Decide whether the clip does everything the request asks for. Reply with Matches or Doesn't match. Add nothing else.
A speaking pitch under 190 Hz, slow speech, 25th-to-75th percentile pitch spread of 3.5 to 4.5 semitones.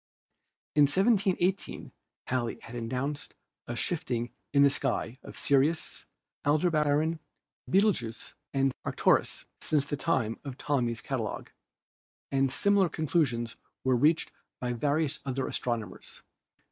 Matches